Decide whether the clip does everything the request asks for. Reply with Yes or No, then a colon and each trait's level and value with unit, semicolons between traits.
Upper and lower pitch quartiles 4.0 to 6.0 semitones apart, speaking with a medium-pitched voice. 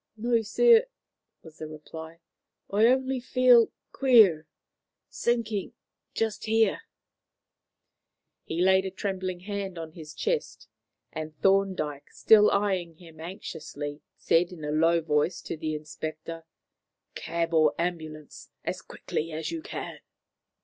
Yes: average, 5.2 semitones; medium, 175 Hz